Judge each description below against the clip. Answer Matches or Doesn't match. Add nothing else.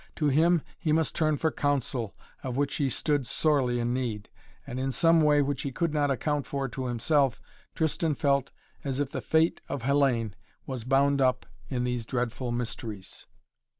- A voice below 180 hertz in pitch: Matches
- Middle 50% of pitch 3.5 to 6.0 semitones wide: Doesn't match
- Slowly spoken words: Doesn't match